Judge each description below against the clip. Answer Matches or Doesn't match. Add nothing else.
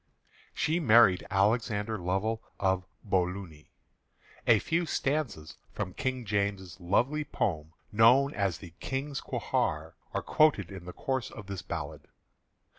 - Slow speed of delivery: Matches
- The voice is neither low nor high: Doesn't match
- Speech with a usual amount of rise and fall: Doesn't match